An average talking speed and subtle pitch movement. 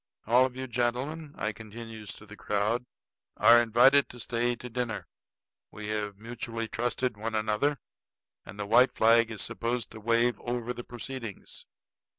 Yes: average, 160 wpm; narrow, 2.1 semitones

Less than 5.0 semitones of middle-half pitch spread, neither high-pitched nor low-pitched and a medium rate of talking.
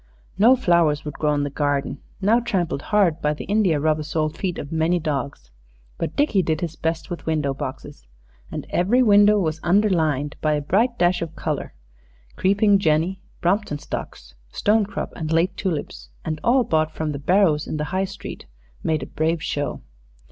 Yes: average, 4.5 semitones; medium, 160 Hz; average, 175 wpm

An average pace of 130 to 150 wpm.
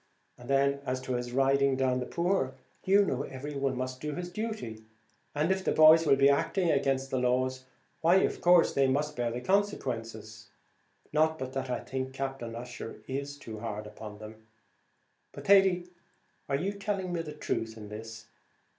No: average, 180 wpm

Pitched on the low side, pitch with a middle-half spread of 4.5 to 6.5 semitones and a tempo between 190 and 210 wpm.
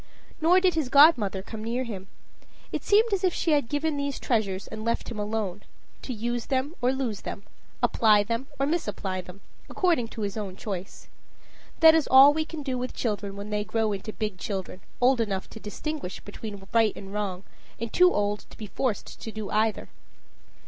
No: high, 225 Hz; average, 5.1 semitones; average, 195 wpm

